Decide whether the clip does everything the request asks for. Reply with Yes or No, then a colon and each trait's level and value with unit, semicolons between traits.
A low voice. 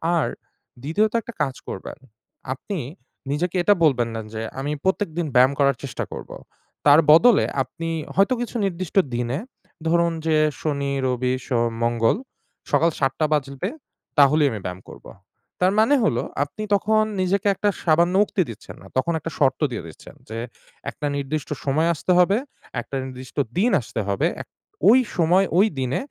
No: medium, 155 Hz